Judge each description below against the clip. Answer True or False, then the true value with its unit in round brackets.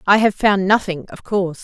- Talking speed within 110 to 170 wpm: False (220 wpm)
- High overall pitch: True (195 Hz)